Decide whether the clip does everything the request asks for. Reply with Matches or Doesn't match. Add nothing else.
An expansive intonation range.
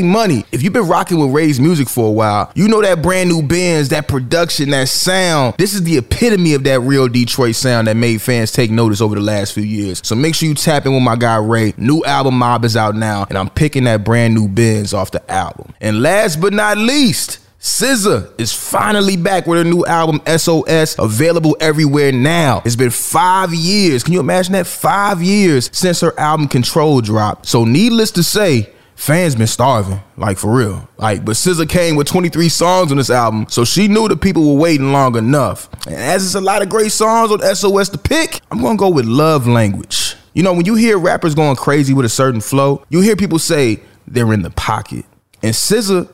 Matches